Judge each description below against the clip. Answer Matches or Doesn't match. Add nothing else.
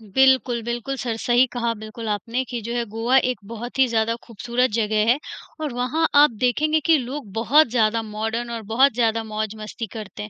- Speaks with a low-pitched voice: Doesn't match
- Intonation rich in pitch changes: Doesn't match